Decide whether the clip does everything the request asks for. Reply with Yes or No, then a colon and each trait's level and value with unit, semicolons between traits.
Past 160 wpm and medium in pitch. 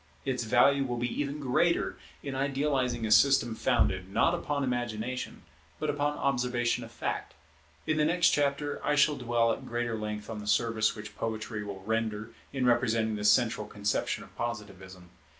No: average, 170 wpm; low, 120 Hz